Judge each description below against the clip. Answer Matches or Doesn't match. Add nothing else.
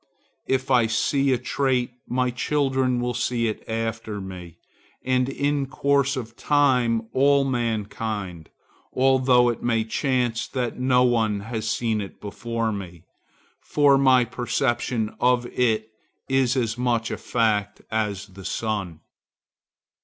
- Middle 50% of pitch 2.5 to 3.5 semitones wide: Matches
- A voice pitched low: Matches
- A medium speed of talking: Doesn't match